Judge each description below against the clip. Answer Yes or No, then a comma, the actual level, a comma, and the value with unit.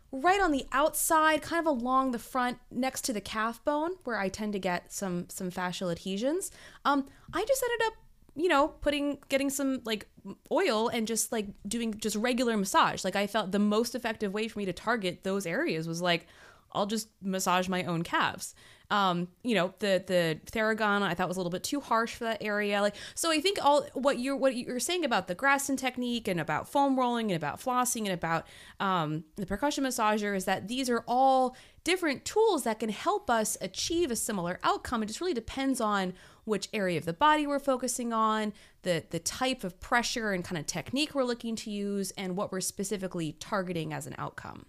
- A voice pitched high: Yes, high, 220 Hz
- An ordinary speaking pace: No, fast, 210 wpm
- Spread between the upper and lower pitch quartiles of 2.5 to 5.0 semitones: No, wide, 5.6 semitones